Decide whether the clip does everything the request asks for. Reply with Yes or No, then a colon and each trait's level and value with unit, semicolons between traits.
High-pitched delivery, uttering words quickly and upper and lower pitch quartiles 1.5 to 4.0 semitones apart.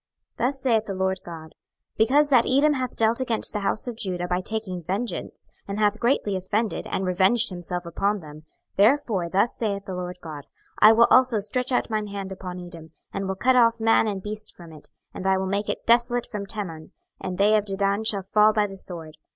Yes: high, 205 Hz; fast, 215 wpm; average, 3.6 semitones